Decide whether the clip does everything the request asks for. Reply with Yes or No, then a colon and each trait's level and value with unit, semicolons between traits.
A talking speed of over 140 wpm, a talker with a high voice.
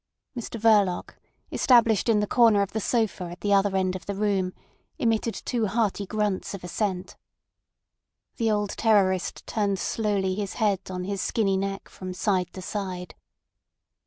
Yes: average, 160 wpm; high, 200 Hz